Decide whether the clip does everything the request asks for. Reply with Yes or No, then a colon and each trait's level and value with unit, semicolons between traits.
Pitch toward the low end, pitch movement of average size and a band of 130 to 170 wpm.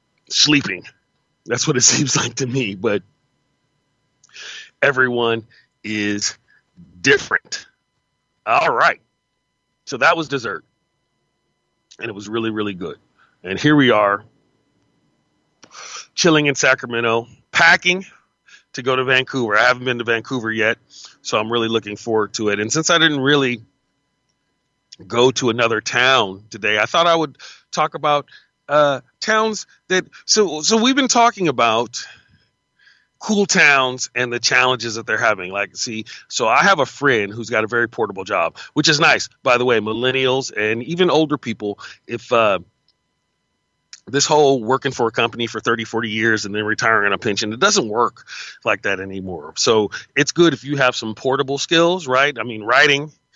Yes: low, 125 Hz; average, 4.7 semitones; average, 160 wpm